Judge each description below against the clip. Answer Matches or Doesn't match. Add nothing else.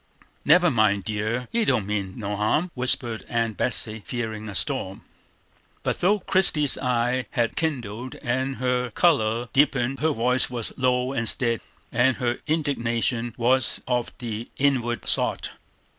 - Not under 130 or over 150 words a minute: Matches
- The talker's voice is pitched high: Doesn't match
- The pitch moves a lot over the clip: Doesn't match